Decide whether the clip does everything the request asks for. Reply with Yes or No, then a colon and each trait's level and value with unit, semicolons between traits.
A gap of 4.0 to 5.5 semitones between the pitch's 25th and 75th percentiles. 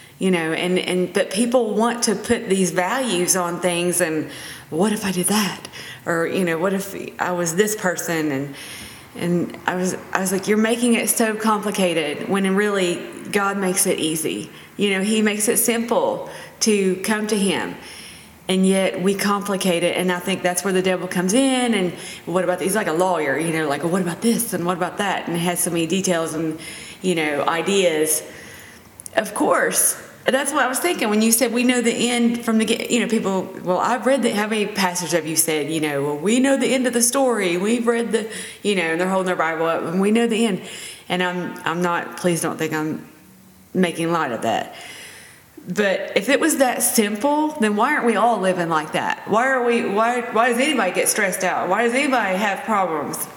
Yes: average, 4.3 semitones